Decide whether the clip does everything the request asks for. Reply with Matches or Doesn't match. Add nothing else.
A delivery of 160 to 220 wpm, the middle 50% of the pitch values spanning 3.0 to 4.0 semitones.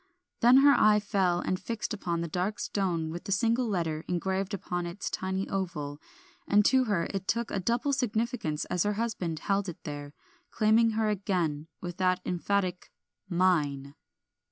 Matches